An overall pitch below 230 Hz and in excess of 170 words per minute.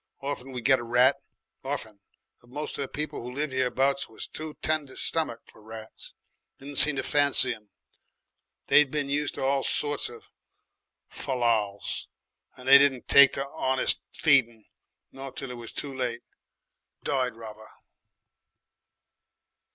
No: low, 135 Hz; average, 145 wpm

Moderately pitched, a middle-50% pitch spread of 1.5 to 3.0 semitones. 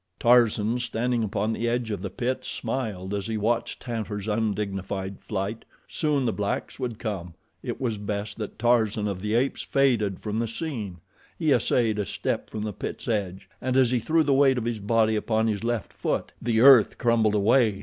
No: low, 110 Hz; average, 2.7 semitones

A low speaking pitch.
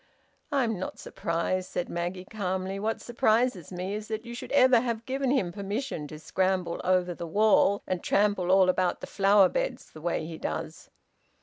No: high, 190 Hz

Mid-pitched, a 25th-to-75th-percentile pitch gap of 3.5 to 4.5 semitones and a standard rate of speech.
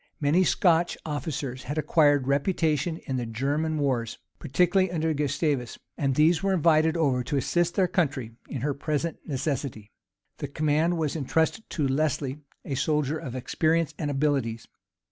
No: medium, 150 Hz; average, 3.0 semitones; average, 150 wpm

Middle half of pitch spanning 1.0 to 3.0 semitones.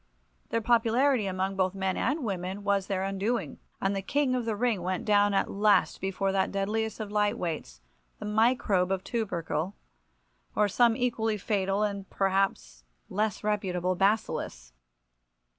Yes: narrow, 2.6 semitones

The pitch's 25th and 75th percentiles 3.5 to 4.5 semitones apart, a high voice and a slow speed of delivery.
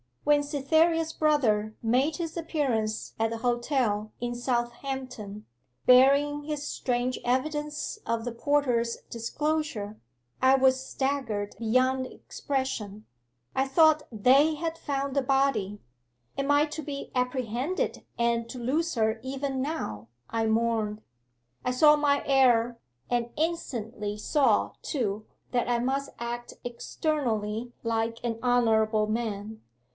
Yes: average, 4.0 semitones; very high, 250 Hz; slow, 120 wpm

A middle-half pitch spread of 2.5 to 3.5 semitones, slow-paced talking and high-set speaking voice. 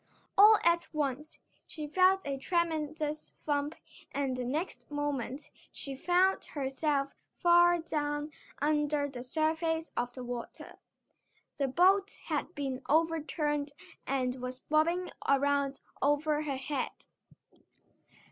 Yes: average, 2.8 semitones; slow, 115 wpm; very high, 295 Hz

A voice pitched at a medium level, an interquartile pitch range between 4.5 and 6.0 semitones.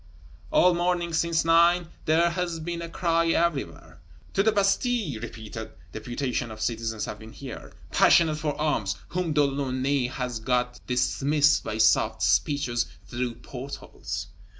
Yes: medium, 145 Hz; wide, 5.5 semitones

